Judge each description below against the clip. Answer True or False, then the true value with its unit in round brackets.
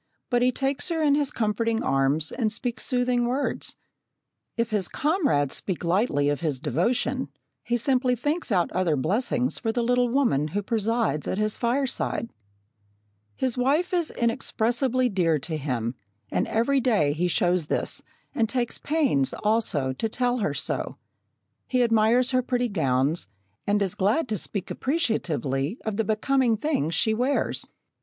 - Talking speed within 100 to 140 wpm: False (155 wpm)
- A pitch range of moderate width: False (6.6 semitones)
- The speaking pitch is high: True (225 Hz)